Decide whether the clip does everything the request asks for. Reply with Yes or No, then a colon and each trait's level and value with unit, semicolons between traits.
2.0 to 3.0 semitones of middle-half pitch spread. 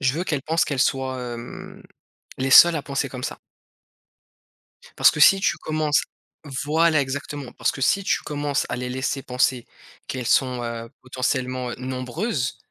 Yes: average, 2.7 semitones